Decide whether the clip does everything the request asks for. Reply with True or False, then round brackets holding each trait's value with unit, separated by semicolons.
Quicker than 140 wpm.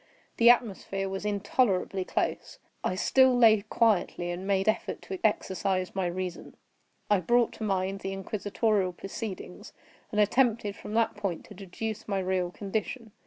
True (150 wpm)